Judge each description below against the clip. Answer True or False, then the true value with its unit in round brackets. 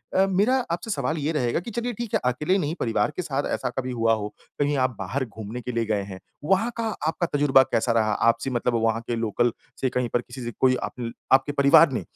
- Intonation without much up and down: False (4.5 semitones)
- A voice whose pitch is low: True (125 Hz)